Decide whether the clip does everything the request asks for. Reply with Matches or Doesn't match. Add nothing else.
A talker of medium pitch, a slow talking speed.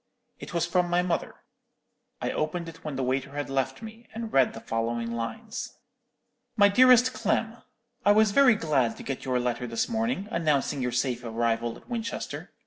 Doesn't match